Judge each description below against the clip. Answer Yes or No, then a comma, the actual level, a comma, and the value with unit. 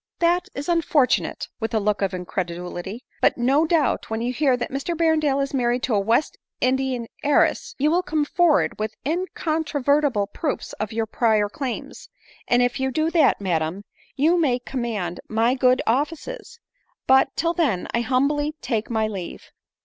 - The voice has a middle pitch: No, very high, 255 Hz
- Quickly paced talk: No, average, 175 wpm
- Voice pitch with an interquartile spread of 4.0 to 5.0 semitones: No, wide, 5.4 semitones